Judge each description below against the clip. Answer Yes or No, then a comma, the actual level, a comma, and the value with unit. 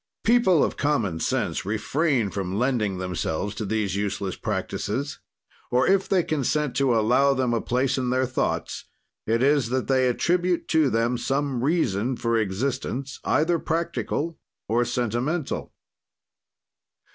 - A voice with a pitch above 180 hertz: No, low, 125 Hz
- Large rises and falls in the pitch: No, average, 4.8 semitones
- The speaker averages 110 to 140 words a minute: Yes, slow, 135 wpm